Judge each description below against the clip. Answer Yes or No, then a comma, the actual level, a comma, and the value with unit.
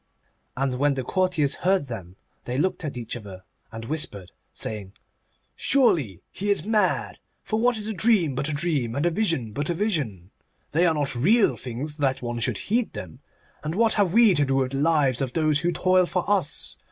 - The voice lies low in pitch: No, medium, 150 Hz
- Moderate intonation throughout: No, wide, 6.9 semitones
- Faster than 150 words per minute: Yes, average, 200 wpm